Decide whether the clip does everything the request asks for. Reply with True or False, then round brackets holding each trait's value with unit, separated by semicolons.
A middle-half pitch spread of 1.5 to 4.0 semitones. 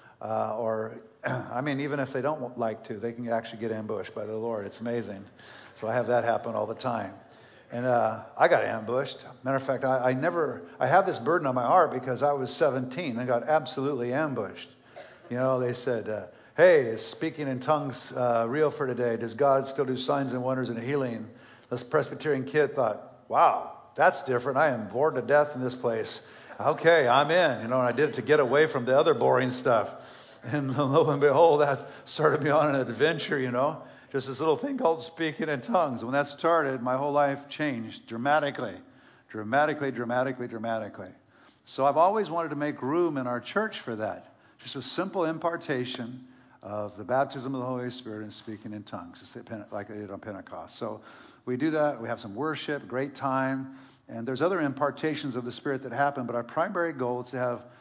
True (3.3 semitones)